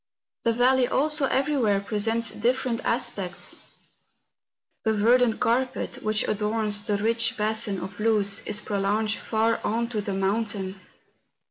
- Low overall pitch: No, high, 220 Hz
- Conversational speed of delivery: No, slow, 125 wpm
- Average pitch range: No, narrow, 2.3 semitones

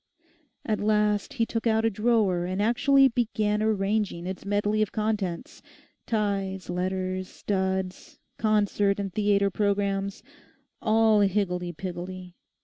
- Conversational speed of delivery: No, slow, 115 wpm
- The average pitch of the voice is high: Yes, high, 205 Hz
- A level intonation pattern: Yes, narrow, 2.3 semitones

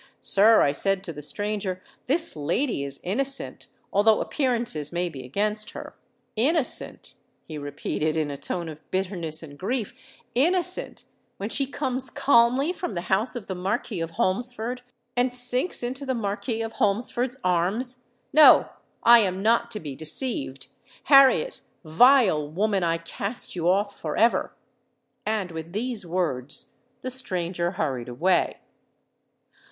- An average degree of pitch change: No, wide, 6.7 semitones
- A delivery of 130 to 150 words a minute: Yes, average, 140 wpm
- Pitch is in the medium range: No, high, 205 Hz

